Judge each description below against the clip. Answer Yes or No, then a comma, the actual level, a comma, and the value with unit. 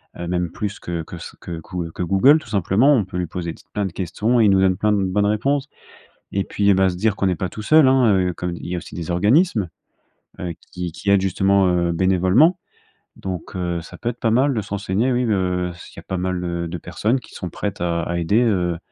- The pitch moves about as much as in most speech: Yes, average, 3.3 semitones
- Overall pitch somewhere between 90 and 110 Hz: Yes, very low, 95 Hz